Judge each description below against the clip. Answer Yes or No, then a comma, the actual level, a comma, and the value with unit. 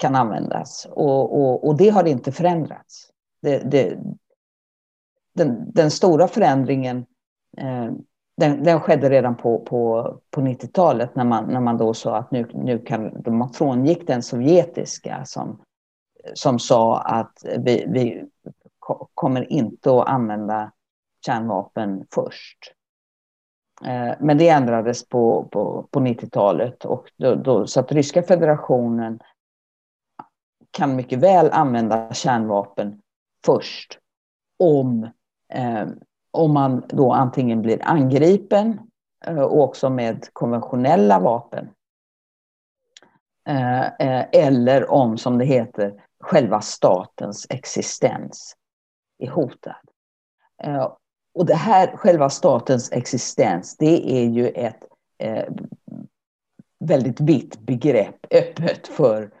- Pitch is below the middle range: Yes, low, 130 Hz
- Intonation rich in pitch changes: No, average, 4.5 semitones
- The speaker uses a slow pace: Yes, slow, 110 wpm